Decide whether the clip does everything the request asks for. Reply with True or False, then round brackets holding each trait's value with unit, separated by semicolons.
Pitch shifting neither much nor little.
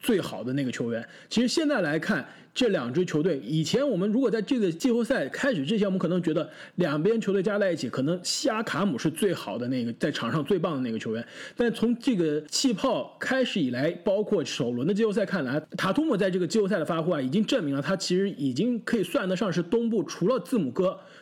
False (6.1 semitones)